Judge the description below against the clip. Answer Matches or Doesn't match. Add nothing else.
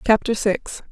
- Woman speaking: Matches